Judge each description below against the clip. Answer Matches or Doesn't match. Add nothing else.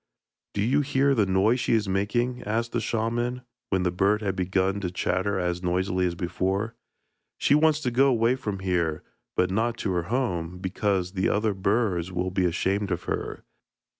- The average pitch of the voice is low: Matches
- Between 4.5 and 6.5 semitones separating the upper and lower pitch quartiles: Doesn't match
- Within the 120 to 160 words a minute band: Doesn't match